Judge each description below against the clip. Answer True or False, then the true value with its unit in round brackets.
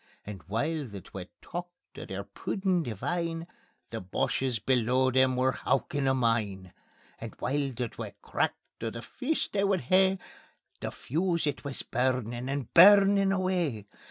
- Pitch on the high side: False (135 Hz)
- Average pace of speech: True (155 wpm)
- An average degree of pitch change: False (7.0 semitones)